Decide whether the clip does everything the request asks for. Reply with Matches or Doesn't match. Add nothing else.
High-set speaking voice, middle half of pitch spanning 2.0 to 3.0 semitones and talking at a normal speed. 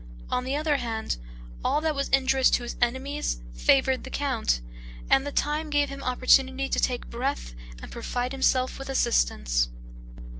Matches